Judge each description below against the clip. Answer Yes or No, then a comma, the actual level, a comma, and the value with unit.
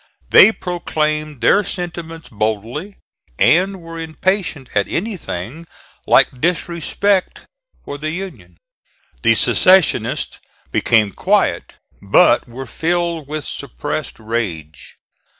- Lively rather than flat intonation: Yes, wide, 6.2 semitones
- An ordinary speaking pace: No, slow, 95 wpm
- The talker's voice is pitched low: No, medium, 155 Hz